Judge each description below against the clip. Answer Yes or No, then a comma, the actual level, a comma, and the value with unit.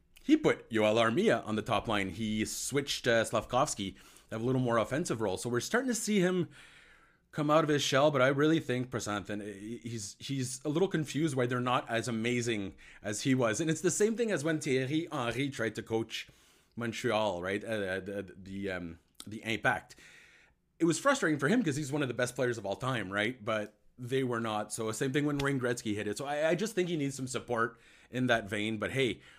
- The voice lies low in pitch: Yes, low, 120 Hz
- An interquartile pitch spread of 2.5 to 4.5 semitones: No, wide, 5.5 semitones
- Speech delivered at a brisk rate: Yes, fast, 225 wpm